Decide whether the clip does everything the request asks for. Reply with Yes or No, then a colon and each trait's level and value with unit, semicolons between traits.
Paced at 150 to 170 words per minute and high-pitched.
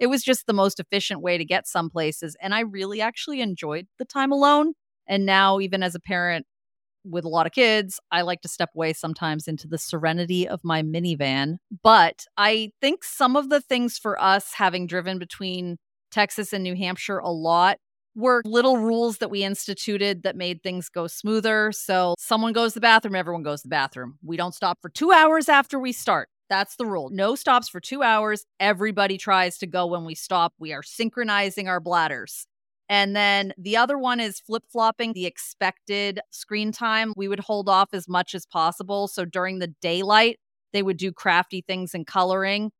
No: average, 200 wpm; high, 195 Hz